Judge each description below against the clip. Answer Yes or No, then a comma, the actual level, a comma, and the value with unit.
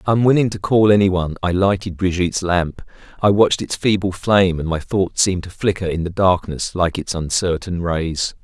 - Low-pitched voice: Yes, very low, 95 Hz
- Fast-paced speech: No, average, 190 wpm